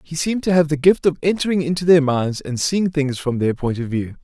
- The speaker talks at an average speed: No, fast, 270 wpm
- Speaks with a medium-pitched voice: Yes, medium, 155 Hz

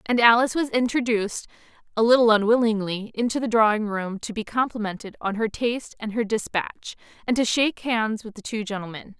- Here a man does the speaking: No, female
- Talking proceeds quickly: No, average, 185 wpm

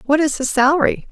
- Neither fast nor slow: No, fast, 215 wpm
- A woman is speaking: Yes, female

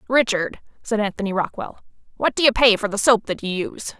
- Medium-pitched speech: No, high, 215 Hz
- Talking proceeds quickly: Yes, fast, 210 wpm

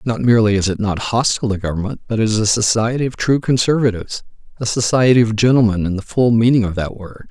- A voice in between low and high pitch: No, low, 110 Hz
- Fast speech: Yes, fast, 215 wpm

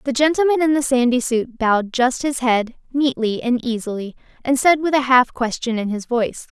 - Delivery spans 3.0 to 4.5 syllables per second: No, 5.4 syllables/s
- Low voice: No, very high, 250 Hz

